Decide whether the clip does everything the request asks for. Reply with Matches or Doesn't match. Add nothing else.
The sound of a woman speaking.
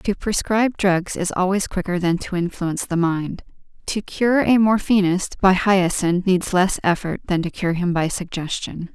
Matches